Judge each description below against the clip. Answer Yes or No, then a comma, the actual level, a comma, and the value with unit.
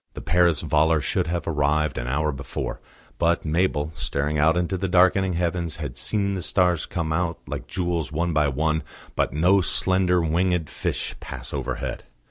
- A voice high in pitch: No, very low, 85 Hz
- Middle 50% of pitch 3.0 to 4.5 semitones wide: No, narrow, 2.6 semitones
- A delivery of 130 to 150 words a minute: No, average, 170 wpm